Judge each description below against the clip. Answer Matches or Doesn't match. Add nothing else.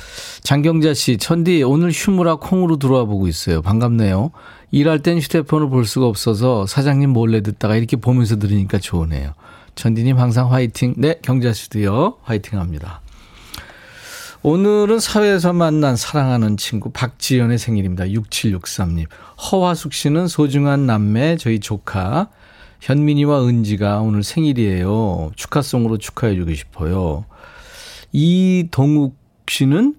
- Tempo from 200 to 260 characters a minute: Doesn't match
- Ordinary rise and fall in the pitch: Doesn't match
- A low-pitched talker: Matches